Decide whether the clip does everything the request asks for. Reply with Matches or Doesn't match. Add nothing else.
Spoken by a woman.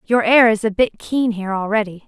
Matches